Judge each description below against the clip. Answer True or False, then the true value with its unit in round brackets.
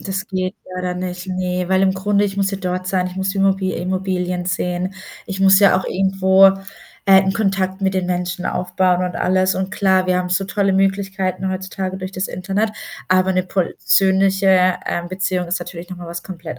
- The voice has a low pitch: False (185 Hz)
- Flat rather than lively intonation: True (1.0 semitones)